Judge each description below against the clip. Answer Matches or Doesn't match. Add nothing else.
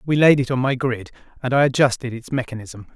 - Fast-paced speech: Matches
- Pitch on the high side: Doesn't match